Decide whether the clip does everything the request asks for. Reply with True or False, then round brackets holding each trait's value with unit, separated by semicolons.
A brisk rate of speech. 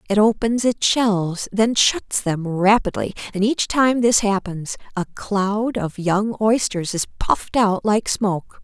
False (160 wpm)